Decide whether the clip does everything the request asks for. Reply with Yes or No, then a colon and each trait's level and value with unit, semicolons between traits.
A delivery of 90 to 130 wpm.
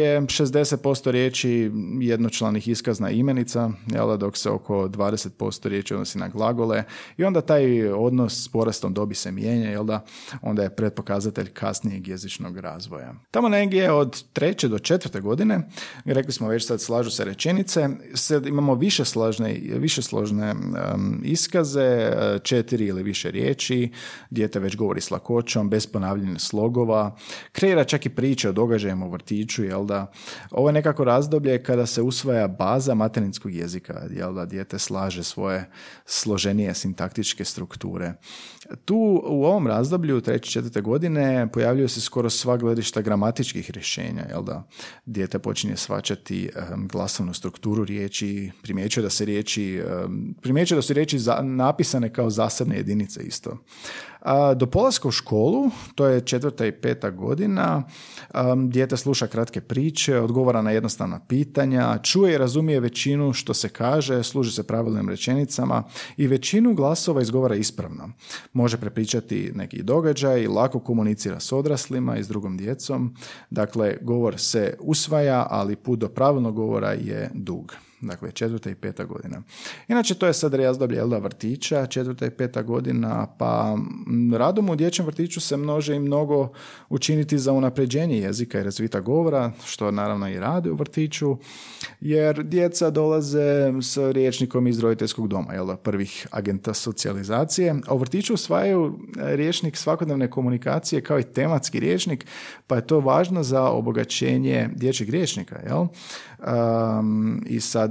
No: average, 140 wpm